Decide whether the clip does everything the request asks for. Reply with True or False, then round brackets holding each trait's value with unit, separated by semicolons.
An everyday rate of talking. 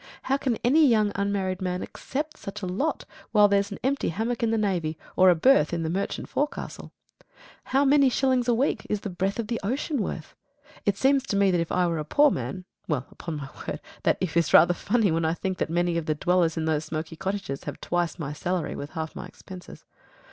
False (225 wpm)